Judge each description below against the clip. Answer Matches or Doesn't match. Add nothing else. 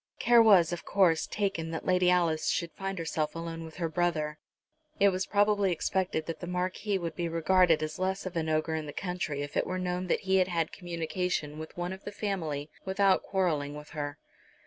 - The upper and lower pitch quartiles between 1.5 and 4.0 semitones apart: Matches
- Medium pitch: Matches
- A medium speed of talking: Doesn't match